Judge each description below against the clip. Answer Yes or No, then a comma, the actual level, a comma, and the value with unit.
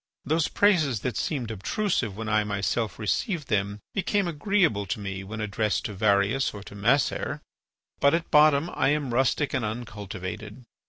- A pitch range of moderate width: No, wide, 6.4 semitones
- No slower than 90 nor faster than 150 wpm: No, average, 160 wpm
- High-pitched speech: No, low, 115 Hz